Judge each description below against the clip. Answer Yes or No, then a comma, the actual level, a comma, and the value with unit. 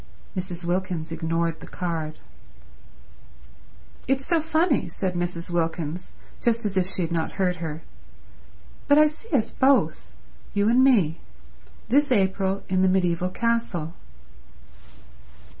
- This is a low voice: No, medium, 185 Hz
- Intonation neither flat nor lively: No, wide, 5.8 semitones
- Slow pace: Yes, slow, 120 wpm